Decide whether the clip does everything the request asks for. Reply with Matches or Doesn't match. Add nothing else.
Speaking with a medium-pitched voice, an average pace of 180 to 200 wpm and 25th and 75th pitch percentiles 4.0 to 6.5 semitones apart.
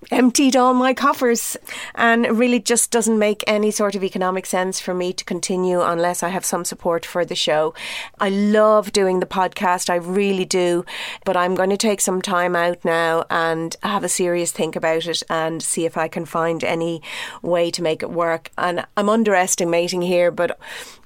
Doesn't match